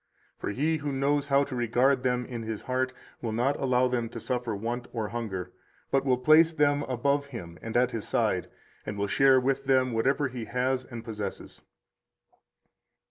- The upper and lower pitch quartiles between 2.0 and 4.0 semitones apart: Yes, average, 2.9 semitones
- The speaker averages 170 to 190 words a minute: Yes, average, 185 wpm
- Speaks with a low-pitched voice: Yes, low, 125 Hz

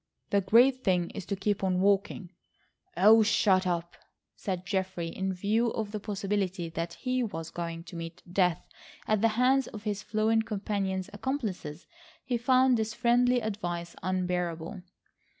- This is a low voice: No, high, 200 Hz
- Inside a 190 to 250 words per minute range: No, average, 150 wpm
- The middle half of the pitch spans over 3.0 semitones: Yes, average, 3.7 semitones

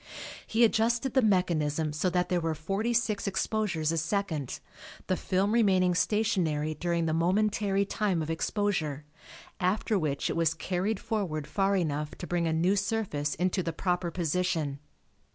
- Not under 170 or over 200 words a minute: No, average, 150 wpm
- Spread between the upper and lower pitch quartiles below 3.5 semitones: No, average, 4.1 semitones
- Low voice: No, medium, 180 Hz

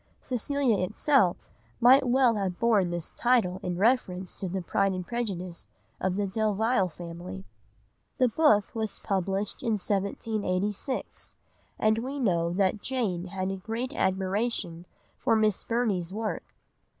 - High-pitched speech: Yes, high, 200 Hz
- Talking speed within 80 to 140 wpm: Yes, slow, 135 wpm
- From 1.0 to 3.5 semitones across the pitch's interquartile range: No, average, 4.2 semitones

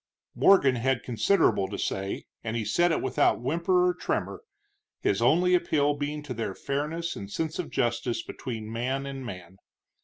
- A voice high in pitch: No, low, 135 Hz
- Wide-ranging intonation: Yes, wide, 6.0 semitones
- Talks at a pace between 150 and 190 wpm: Yes, average, 165 wpm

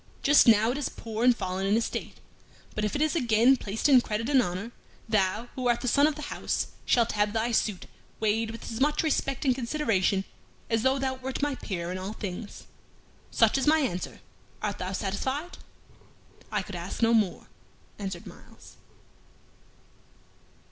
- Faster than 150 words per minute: Yes, average, 175 wpm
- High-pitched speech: Yes, high, 230 Hz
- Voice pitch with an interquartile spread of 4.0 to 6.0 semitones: Yes, average, 4.5 semitones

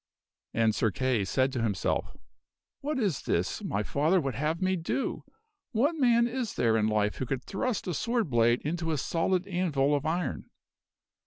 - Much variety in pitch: Yes, wide, 7.9 semitones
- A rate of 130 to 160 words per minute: No, average, 180 wpm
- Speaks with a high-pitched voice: No, medium, 155 Hz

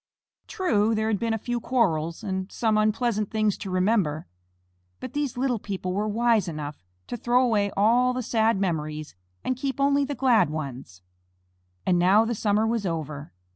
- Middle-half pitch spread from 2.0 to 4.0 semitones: No, average, 4.7 semitones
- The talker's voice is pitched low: No, high, 215 Hz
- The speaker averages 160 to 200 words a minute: Yes, average, 175 wpm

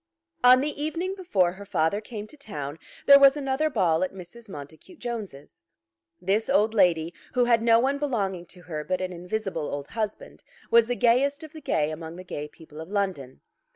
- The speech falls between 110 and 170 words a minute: No, average, 190 wpm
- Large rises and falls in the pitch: Yes, wide, 6.8 semitones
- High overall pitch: Yes, high, 205 Hz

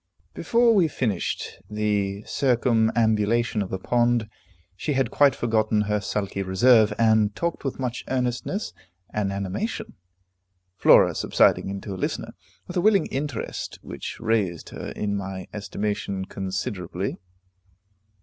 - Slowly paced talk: Yes, slow, 125 wpm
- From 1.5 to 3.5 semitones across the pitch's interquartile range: No, average, 3.9 semitones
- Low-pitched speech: Yes, low, 110 Hz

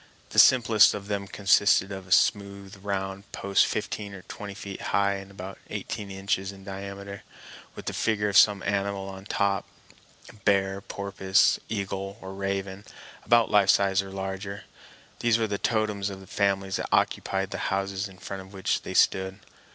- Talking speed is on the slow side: No, average, 170 wpm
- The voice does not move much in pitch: Yes, narrow, 0.7 semitones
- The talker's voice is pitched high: No, low, 100 Hz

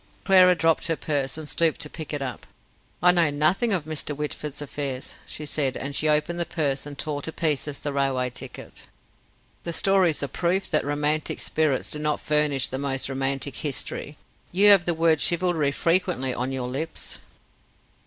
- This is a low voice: No, medium, 150 Hz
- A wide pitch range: No, average, 3.0 semitones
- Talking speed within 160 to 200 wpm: Yes, average, 180 wpm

